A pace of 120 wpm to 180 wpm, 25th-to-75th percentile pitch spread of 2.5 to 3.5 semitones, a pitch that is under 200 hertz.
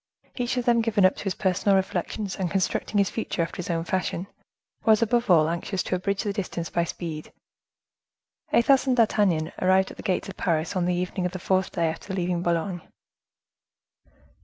No: average, 190 wpm; average, 3.0 semitones; medium, 185 Hz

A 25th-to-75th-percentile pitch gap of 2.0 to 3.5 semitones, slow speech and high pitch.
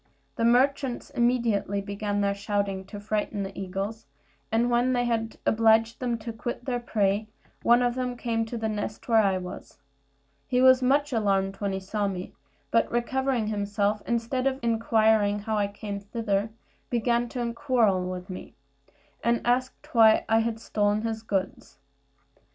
No: average, 2.9 semitones; average, 160 wpm; high, 225 Hz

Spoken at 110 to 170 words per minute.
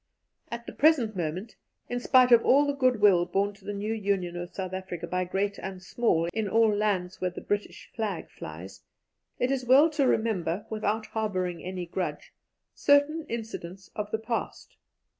No: average, 180 wpm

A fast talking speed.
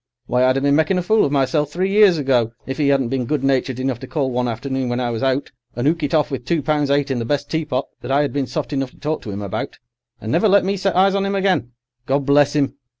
Yes: fast, 285 wpm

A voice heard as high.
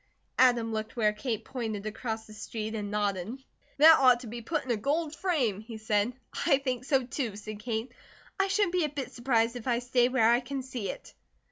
Yes: high, 240 Hz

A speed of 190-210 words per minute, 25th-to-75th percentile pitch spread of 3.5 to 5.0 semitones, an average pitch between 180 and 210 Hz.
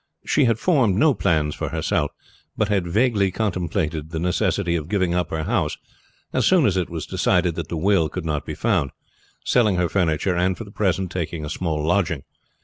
No: average, 200 wpm; average, 3.8 semitones; very low, 90 Hz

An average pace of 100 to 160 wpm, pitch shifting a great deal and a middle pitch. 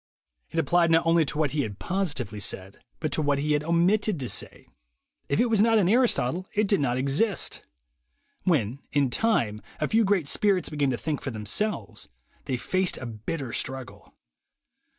No: average, 185 wpm; wide, 6.6 semitones; medium, 150 Hz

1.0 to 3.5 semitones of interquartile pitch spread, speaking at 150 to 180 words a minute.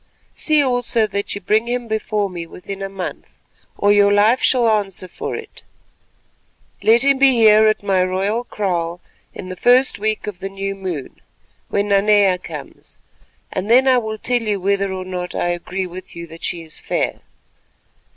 Yes: average, 3.2 semitones; average, 170 wpm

